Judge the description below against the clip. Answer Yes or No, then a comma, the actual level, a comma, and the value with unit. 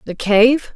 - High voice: Yes, high, 235 Hz